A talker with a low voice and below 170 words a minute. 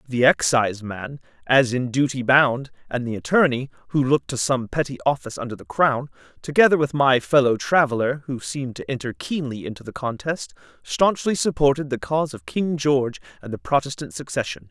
No: low, 130 Hz; average, 175 wpm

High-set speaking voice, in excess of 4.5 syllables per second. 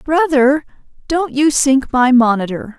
No: very high, 275 Hz; 4.0 syllables/s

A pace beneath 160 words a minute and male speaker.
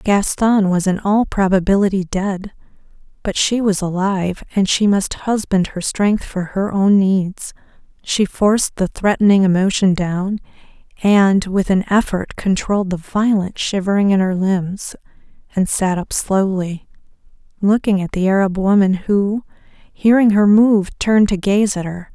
No: average, 150 wpm; female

